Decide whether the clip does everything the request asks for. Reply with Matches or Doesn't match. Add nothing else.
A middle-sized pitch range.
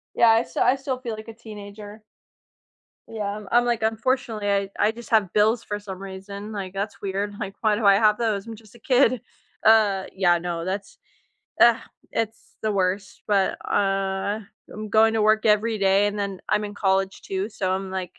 Doesn't match